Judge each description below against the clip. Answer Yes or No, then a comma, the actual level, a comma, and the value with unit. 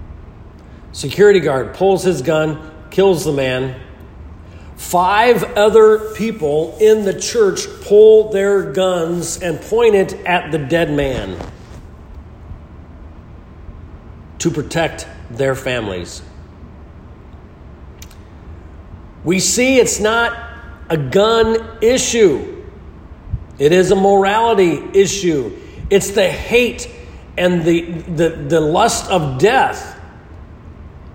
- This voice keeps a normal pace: No, slow, 95 wpm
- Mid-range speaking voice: Yes, medium, 150 Hz